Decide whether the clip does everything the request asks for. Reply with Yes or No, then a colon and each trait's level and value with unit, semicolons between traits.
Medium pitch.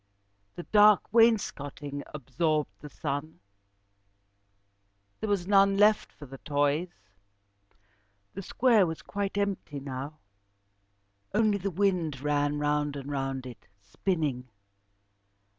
Yes: medium, 155 Hz